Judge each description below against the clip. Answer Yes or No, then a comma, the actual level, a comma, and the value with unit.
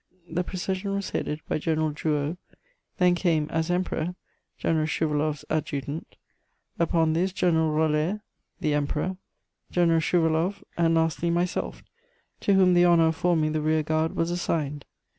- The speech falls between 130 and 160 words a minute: Yes, average, 140 wpm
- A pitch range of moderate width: No, narrow, 2.3 semitones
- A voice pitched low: No, medium, 160 Hz